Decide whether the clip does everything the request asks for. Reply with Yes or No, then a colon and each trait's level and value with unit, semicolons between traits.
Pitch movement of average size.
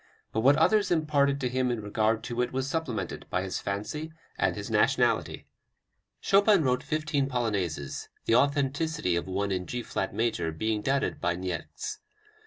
No: wide, 6.1 semitones